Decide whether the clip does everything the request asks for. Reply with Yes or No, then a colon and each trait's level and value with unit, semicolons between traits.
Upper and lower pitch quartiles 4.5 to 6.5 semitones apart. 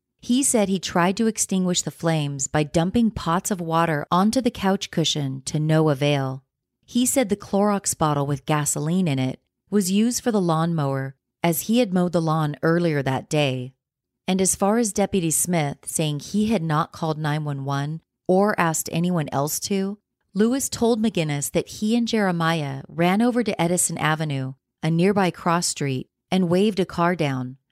Yes: average, 5.2 semitones